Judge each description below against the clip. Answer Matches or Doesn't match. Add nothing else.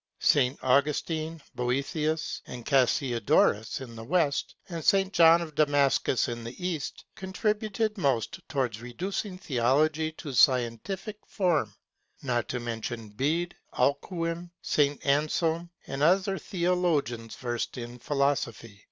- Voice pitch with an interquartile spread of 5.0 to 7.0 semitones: Matches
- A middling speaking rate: Doesn't match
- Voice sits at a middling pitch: Matches